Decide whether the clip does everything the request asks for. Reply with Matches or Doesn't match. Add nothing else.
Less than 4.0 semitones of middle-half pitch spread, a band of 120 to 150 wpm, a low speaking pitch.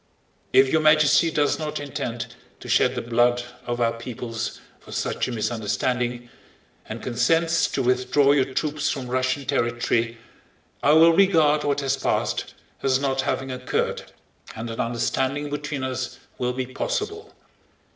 Matches